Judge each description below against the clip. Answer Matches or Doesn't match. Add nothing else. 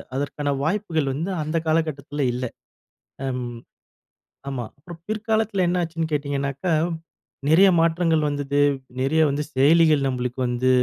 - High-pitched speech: Doesn't match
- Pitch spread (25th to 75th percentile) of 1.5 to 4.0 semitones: Matches